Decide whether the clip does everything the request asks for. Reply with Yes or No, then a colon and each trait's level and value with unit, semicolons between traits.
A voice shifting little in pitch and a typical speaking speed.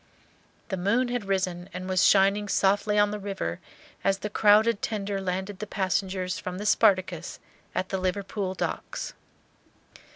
Yes: narrow, 1.9 semitones; average, 150 wpm